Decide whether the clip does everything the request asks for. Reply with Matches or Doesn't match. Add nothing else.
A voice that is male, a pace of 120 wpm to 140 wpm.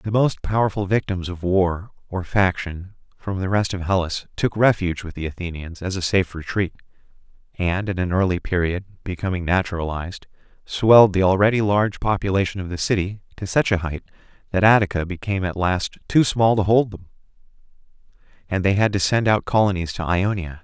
Doesn't match